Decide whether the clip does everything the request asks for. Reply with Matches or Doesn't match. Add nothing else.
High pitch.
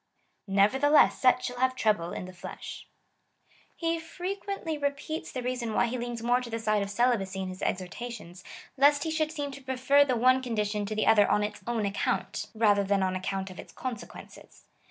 Matches